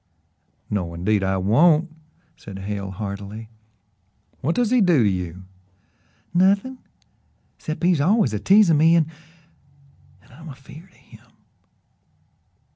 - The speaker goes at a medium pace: No, slow, 120 wpm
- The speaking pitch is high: No, medium, 140 Hz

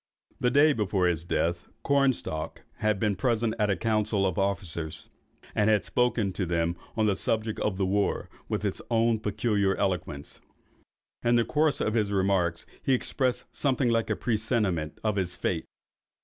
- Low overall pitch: Yes, low, 105 Hz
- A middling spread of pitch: Yes, average, 3.7 semitones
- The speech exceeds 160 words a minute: Yes, average, 170 wpm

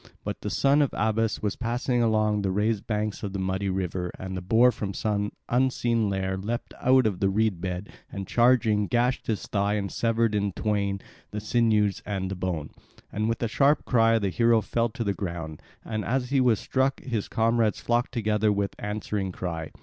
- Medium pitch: No, low, 105 Hz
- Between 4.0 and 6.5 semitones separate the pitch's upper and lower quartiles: No, average, 3.0 semitones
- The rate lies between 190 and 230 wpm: Yes, average, 195 wpm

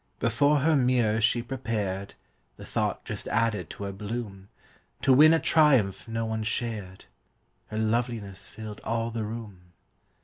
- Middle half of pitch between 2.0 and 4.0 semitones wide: Yes, average, 2.7 semitones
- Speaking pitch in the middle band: No, low, 115 Hz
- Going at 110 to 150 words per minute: Yes, average, 145 wpm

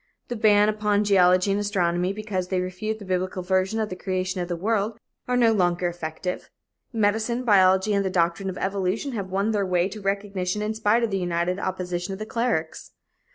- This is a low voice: No, high, 195 Hz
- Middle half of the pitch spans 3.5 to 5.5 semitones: No, average, 2.7 semitones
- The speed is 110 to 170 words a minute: No, average, 200 wpm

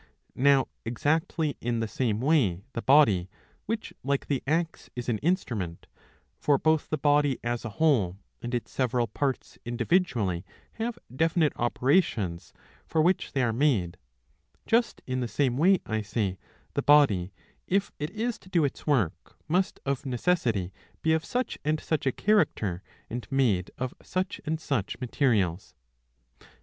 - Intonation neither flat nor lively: No, wide, 6.2 semitones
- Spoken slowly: No, average, 160 wpm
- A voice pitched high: No, low, 135 Hz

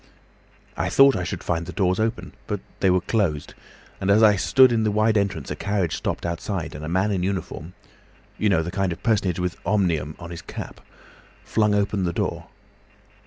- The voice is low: Yes, very low, 95 Hz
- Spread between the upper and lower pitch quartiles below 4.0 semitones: Yes, average, 3.4 semitones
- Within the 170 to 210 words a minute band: Yes, average, 195 wpm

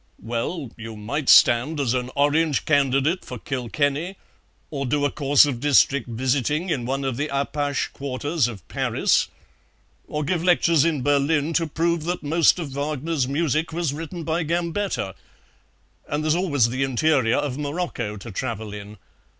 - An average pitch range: Yes, average, 3.9 semitones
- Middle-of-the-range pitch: Yes, medium, 145 Hz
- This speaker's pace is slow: No, average, 160 wpm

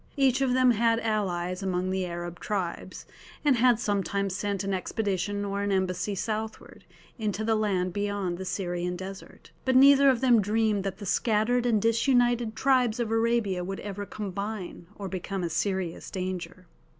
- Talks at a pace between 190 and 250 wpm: No, average, 165 wpm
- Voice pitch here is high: Yes, high, 205 Hz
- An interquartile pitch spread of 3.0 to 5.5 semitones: Yes, average, 3.4 semitones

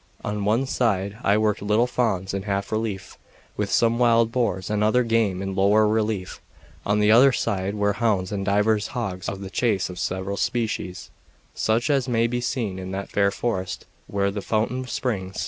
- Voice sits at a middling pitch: No, low, 105 Hz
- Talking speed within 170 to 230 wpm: Yes, average, 185 wpm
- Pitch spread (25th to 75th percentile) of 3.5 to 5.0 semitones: No, average, 2.9 semitones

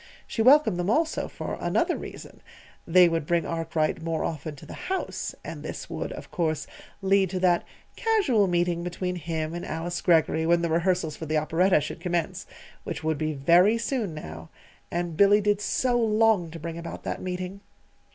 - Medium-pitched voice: Yes, medium, 175 Hz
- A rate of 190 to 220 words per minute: No, average, 180 wpm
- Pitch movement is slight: No, average, 3.4 semitones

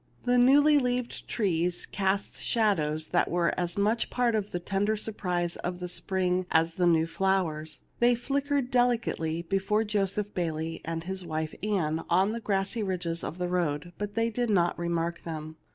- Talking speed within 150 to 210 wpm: Yes, average, 185 wpm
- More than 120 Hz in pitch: Yes, medium, 185 Hz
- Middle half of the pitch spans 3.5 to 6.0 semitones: Yes, average, 4.3 semitones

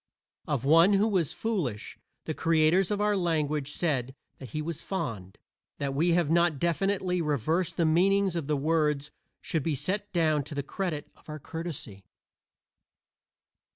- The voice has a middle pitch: Yes, medium, 160 Hz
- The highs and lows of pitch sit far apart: No, average, 3.5 semitones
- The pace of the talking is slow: No, average, 155 wpm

